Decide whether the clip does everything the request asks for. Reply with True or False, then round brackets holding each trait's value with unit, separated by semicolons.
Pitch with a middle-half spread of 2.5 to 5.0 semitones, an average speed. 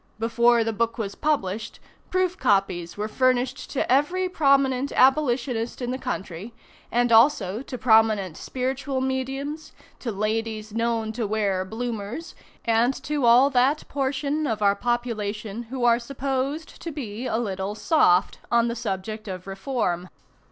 True (3.8 semitones; 145 wpm)